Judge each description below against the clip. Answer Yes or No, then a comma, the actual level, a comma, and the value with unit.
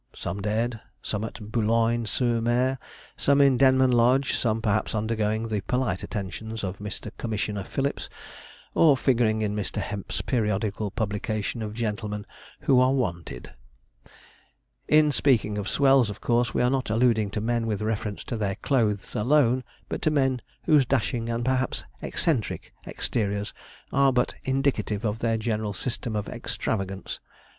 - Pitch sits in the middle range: No, low, 115 Hz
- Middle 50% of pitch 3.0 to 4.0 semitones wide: Yes, average, 3.3 semitones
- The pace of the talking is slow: No, average, 150 wpm